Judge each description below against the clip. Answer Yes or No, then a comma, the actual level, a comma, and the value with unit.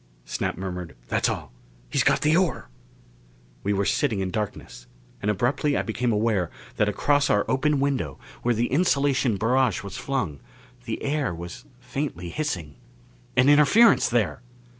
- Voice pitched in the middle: No, low, 120 Hz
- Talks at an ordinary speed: Yes, average, 155 wpm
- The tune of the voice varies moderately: No, wide, 6.6 semitones